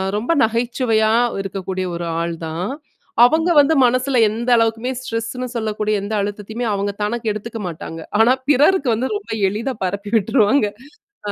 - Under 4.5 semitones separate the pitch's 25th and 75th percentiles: Yes, average, 3.7 semitones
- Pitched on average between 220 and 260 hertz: Yes, high, 225 Hz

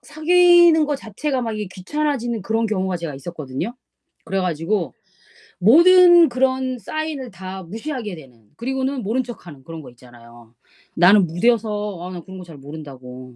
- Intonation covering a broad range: Yes, wide, 8.0 semitones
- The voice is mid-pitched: No, high, 205 Hz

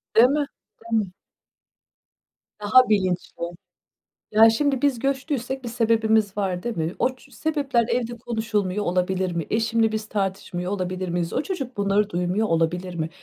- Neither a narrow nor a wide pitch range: Yes, average, 4.6 semitones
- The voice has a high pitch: Yes, high, 215 Hz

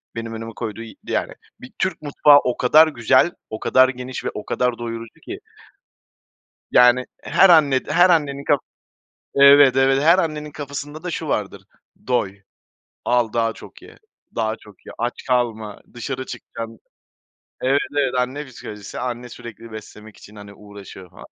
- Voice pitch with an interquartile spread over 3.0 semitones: Yes, average, 4.0 semitones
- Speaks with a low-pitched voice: Yes, low, 125 Hz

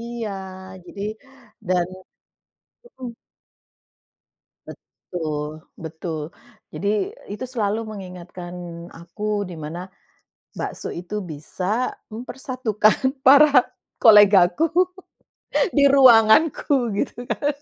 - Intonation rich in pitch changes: Yes, wide, 6.1 semitones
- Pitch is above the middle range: Yes, high, 210 Hz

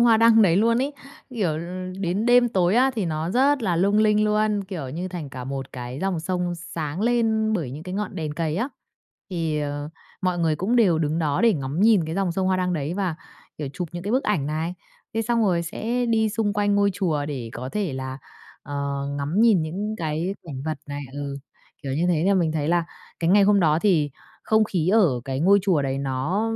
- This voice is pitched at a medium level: Yes, medium, 180 Hz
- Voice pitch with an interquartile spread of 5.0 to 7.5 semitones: Yes, wide, 5.6 semitones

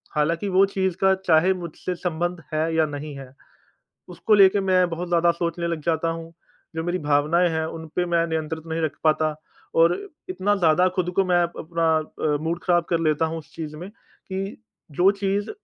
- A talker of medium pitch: Yes, medium, 170 Hz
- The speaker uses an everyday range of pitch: No, narrow, 2.2 semitones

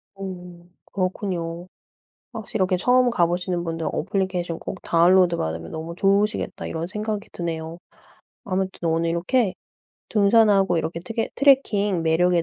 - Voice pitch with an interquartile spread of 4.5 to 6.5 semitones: No, average, 3.0 semitones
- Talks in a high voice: No, medium, 180 Hz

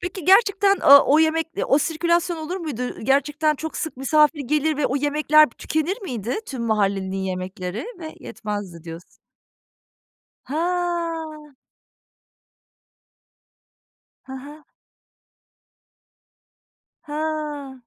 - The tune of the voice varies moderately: Yes, average, 4.2 semitones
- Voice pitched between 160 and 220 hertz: No, very high, 300 Hz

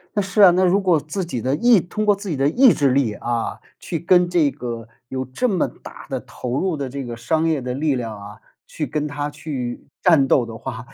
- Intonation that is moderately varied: No, wide, 6.0 semitones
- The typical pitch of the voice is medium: Yes, medium, 145 Hz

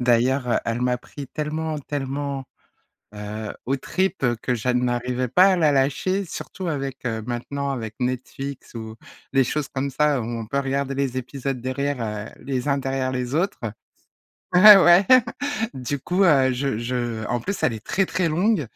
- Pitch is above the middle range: No, low, 135 Hz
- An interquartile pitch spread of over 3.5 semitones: No, average, 3.0 semitones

